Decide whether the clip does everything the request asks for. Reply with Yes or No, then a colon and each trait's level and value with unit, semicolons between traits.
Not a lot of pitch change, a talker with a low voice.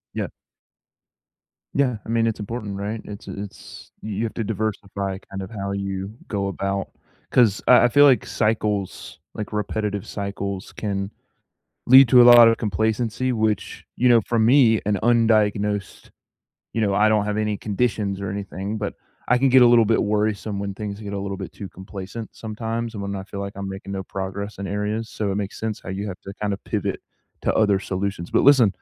Yes: narrow, 2.2 semitones; low, 105 Hz